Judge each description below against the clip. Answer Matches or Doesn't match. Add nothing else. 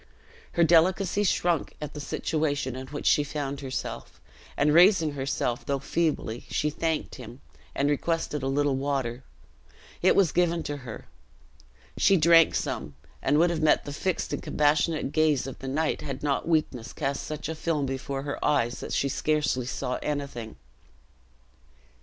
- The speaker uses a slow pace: Doesn't match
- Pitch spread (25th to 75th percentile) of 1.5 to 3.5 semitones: Matches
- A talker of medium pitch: Matches